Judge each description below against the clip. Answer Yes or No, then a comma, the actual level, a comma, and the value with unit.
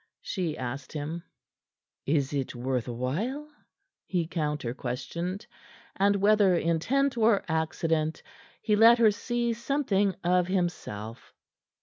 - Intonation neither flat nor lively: No, wide, 6.4 semitones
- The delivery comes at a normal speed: No, slow, 110 wpm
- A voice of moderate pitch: Yes, medium, 175 Hz